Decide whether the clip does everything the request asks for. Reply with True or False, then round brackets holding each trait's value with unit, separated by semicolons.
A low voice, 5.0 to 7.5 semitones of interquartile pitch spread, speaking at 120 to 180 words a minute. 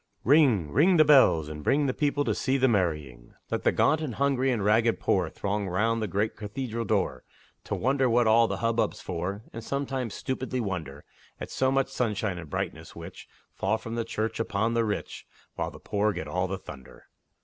False (110 Hz; 5.3 semitones; 200 wpm)